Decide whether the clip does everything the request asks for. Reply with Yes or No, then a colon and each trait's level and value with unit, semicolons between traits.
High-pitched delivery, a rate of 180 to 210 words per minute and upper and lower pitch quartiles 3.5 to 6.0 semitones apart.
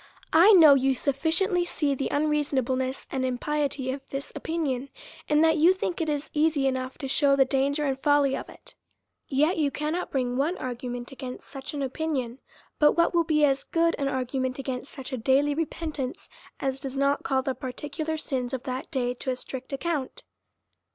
No: very high, 275 Hz; average, 195 wpm; average, 2.7 semitones